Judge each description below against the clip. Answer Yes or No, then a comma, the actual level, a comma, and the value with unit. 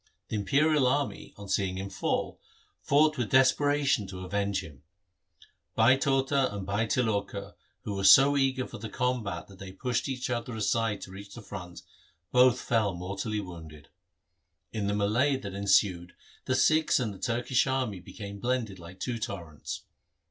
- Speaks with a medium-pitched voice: No, low, 105 Hz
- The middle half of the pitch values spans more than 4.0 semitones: Yes, average, 4.8 semitones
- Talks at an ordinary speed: Yes, average, 160 wpm